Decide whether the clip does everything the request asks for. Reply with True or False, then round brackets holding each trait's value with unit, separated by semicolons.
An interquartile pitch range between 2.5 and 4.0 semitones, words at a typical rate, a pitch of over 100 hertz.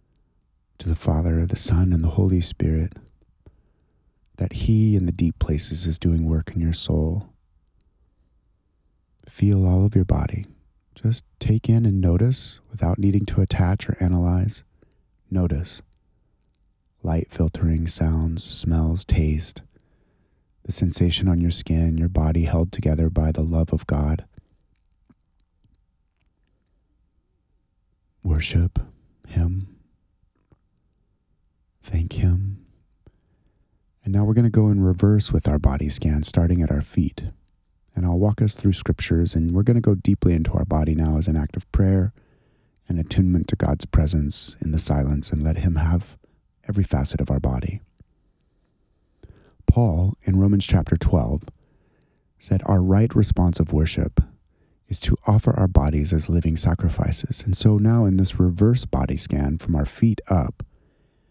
False (3.7 semitones; 145 wpm; 90 Hz)